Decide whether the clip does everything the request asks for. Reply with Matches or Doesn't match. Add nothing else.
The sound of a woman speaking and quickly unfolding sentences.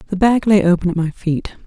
Matches